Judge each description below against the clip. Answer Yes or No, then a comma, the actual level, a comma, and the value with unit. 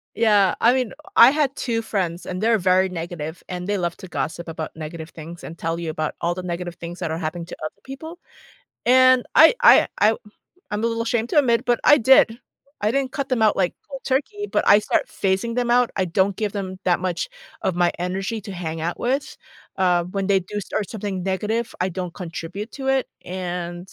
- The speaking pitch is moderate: No, high, 195 Hz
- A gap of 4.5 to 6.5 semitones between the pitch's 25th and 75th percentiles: Yes, average, 5.2 semitones